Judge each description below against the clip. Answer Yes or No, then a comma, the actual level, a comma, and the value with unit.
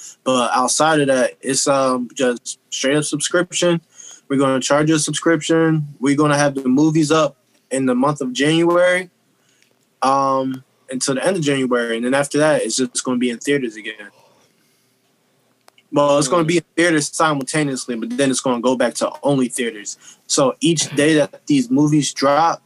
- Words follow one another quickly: No, average, 175 wpm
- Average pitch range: Yes, average, 3.3 semitones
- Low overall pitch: No, medium, 145 Hz